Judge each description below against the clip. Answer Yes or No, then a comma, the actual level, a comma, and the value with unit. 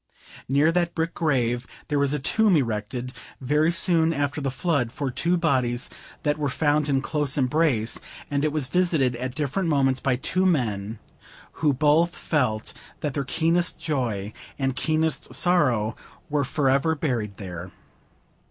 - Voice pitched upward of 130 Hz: Yes, medium, 140 Hz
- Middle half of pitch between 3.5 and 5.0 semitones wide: Yes, average, 4.1 semitones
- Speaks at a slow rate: No, average, 150 wpm